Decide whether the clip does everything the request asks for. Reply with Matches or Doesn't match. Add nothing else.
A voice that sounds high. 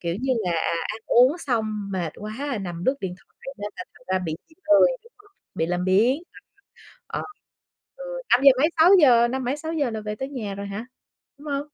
Matches